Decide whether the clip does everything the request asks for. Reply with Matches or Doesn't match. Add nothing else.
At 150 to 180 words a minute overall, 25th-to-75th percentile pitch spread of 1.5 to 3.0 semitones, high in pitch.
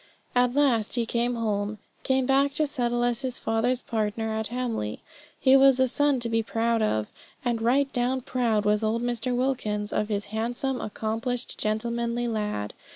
Matches